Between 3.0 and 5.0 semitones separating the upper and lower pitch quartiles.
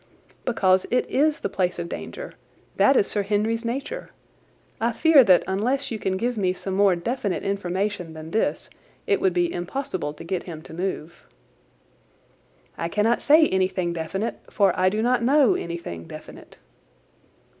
No: wide, 5.5 semitones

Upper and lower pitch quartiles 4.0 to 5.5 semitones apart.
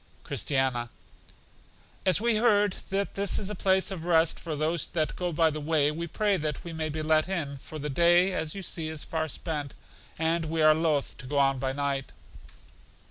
No: average, 3.0 semitones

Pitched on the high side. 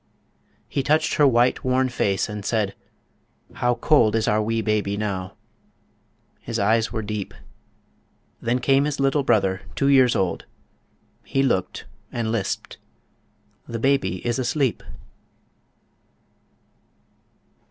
No: low, 115 Hz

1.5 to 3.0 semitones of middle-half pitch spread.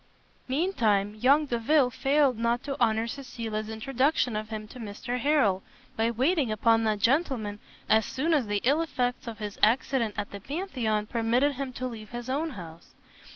No: average, 4.0 semitones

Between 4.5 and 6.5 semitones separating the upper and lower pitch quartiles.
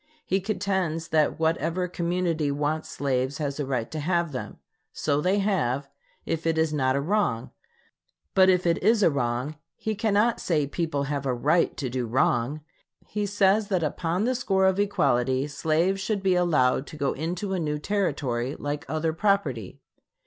Yes: average, 5.2 semitones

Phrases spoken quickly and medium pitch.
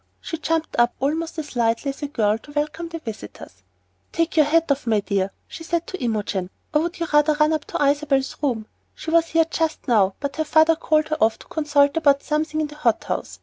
No: fast, 230 wpm; very high, 300 Hz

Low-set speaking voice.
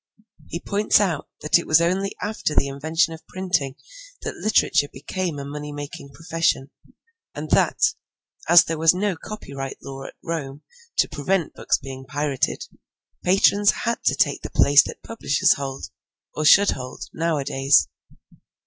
No: medium, 155 Hz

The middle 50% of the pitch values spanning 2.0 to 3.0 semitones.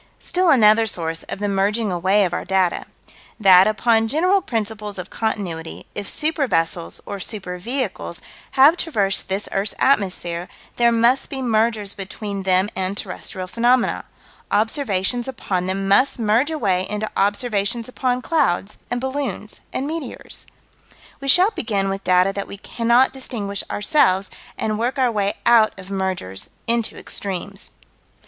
No: average, 4.1 semitones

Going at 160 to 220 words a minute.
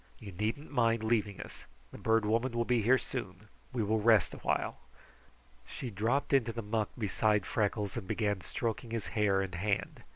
Yes: average, 175 wpm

